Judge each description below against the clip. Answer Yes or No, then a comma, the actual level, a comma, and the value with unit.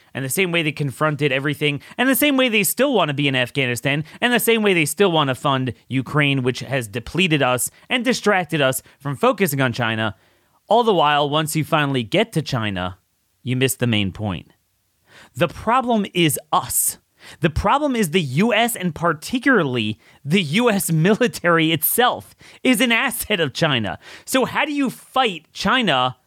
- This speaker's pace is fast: No, average, 180 wpm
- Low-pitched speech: No, medium, 155 Hz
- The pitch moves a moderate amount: No, wide, 8.7 semitones